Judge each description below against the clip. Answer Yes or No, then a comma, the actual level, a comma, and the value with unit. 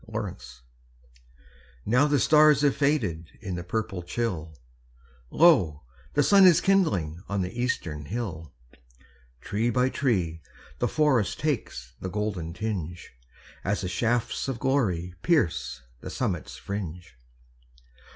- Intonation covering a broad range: Yes, wide, 7.4 semitones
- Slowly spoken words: Yes, slow, 125 wpm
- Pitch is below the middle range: Yes, low, 105 Hz